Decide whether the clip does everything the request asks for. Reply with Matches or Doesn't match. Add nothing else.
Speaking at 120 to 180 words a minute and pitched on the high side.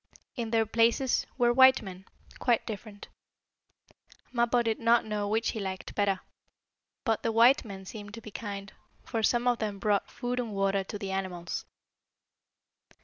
Matches